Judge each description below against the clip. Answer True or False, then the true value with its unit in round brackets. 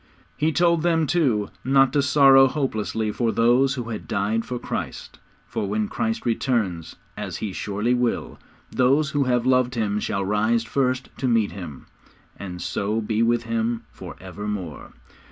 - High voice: False (115 Hz)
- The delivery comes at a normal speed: True (160 wpm)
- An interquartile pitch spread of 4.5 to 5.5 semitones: False (3.9 semitones)